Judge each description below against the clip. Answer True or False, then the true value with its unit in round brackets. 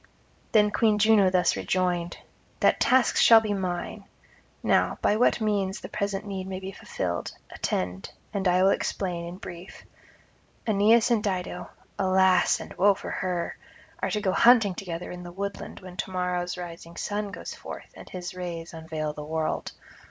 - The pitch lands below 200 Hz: True (185 Hz)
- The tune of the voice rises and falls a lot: False (2.6 semitones)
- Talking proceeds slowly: False (165 wpm)